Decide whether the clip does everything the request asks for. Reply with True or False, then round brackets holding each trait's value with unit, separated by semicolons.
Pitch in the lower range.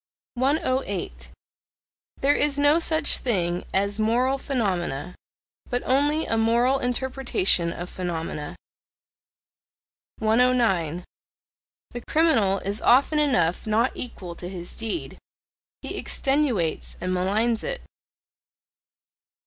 False (225 Hz)